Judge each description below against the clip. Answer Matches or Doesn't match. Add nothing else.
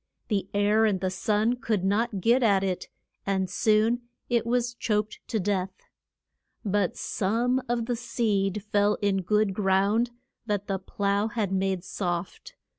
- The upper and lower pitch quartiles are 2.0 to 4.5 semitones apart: Matches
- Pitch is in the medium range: Doesn't match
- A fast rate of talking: Doesn't match